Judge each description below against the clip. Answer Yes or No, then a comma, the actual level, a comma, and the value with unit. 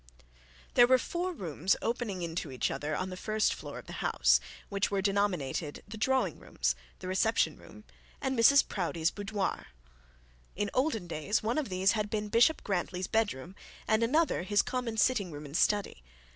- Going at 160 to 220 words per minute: Yes, average, 175 wpm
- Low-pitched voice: No, high, 205 Hz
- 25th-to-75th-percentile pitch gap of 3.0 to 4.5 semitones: Yes, average, 4.2 semitones